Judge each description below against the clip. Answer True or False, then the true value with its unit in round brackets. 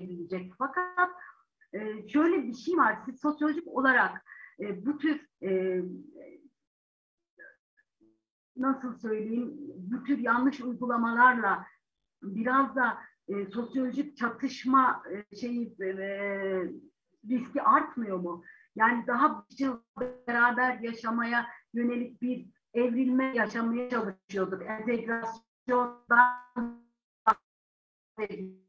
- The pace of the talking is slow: True (75 wpm)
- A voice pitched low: False (240 Hz)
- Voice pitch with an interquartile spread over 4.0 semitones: False (3.7 semitones)